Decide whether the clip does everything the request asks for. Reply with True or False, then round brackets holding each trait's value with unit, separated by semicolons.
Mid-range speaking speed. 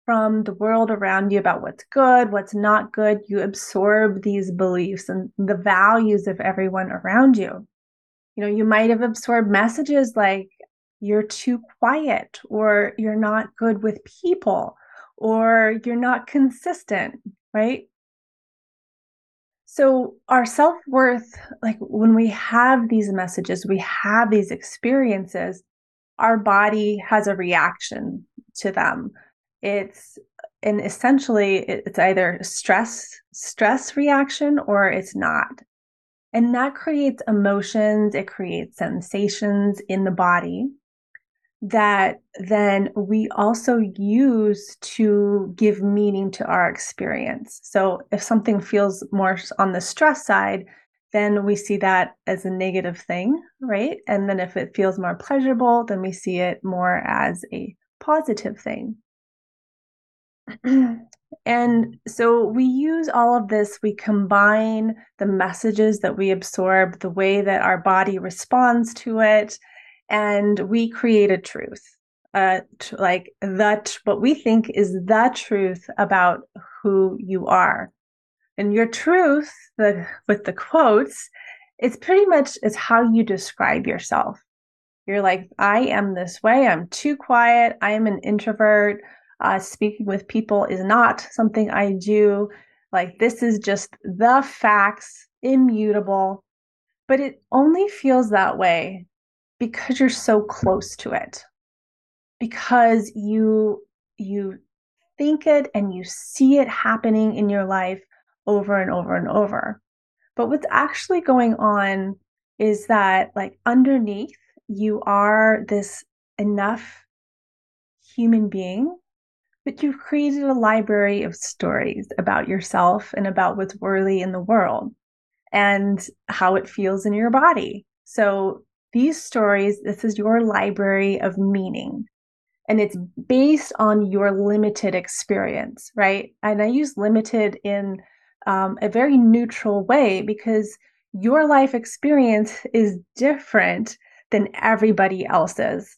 False (130 wpm)